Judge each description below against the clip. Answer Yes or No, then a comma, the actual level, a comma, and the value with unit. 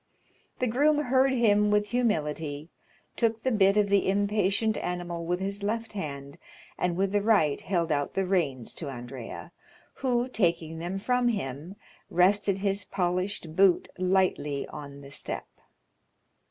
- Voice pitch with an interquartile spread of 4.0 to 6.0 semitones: Yes, average, 4.4 semitones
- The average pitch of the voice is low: No, high, 190 Hz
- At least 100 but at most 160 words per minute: Yes, average, 145 wpm